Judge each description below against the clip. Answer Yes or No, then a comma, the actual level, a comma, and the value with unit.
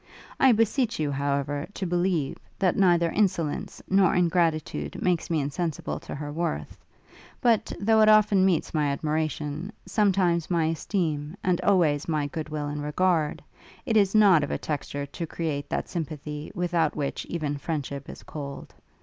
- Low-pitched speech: No, medium, 165 Hz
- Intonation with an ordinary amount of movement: Yes, average, 4.1 semitones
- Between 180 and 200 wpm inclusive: No, average, 160 wpm